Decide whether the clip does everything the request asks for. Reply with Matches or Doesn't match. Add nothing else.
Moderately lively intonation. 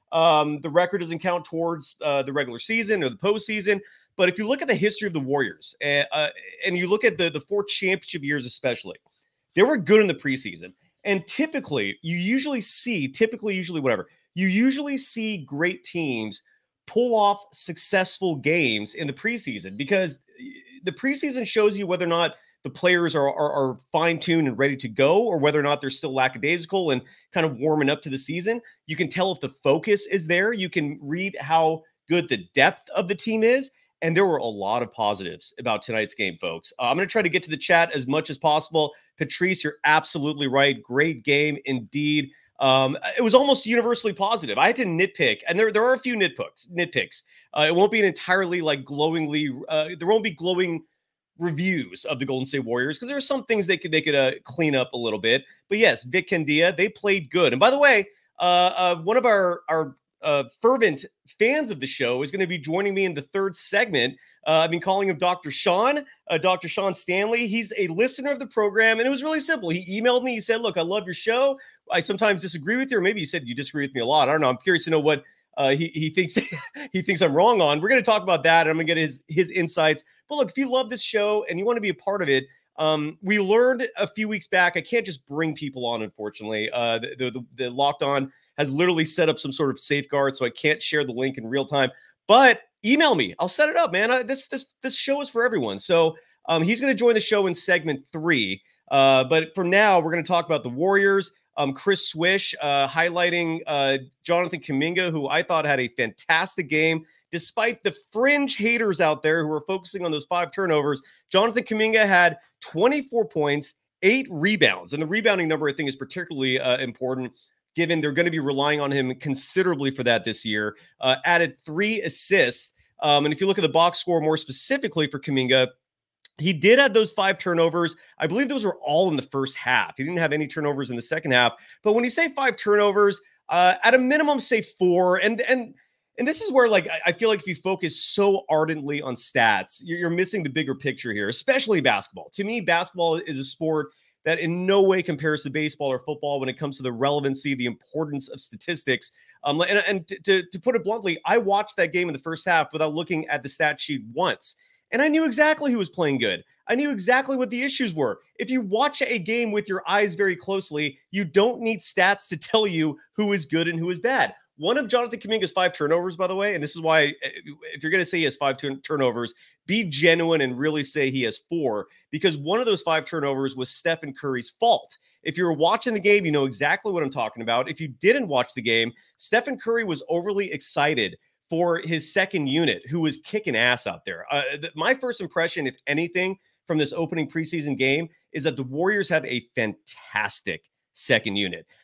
Doesn't match